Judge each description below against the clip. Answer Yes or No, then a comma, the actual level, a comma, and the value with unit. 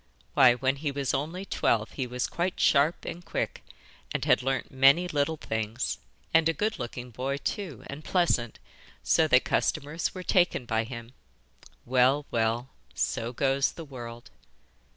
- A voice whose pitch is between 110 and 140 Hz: Yes, low, 135 Hz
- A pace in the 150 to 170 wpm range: Yes, average, 155 wpm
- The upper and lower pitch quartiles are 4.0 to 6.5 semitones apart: Yes, average, 4.7 semitones